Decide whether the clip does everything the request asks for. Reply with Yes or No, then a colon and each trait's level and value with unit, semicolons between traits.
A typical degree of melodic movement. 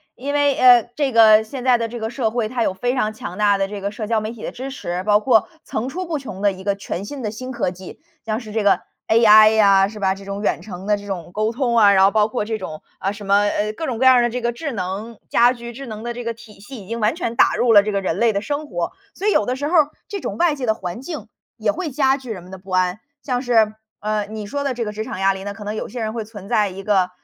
Yes: average, 3.4 semitones